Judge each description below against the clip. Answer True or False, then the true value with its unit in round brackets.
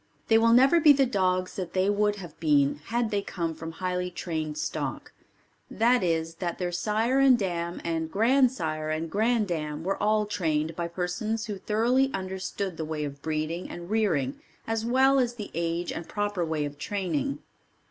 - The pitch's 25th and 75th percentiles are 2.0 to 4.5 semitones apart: False (5.3 semitones)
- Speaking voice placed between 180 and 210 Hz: True (185 Hz)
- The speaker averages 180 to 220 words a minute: True (185 wpm)